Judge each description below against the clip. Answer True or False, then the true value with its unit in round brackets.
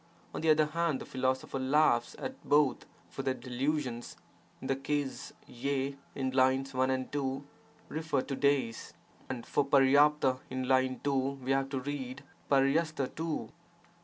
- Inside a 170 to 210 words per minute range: False (155 wpm)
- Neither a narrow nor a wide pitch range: False (1.9 semitones)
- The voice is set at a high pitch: False (135 Hz)